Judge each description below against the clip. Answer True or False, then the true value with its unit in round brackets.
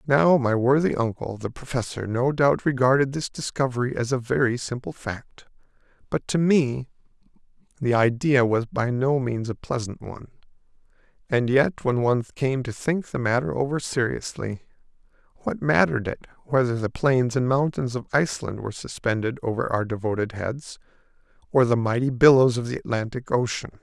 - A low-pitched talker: True (125 Hz)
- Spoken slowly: False (160 wpm)